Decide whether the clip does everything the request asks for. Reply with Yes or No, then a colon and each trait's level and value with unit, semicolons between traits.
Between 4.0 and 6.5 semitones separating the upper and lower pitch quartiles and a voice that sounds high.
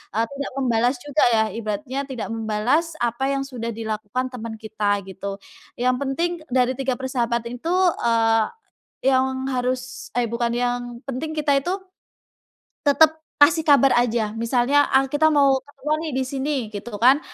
No: average, 3.2 semitones; very high, 250 Hz